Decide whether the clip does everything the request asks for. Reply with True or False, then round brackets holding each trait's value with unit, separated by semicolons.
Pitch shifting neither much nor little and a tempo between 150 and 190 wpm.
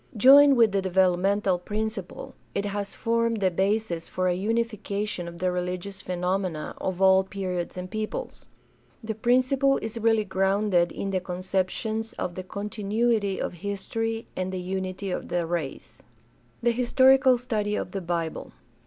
True (3.4 semitones; 155 wpm)